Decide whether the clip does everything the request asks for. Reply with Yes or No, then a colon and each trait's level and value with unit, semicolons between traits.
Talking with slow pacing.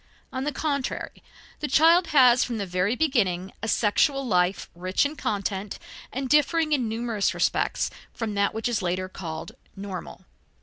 No: average, 160 wpm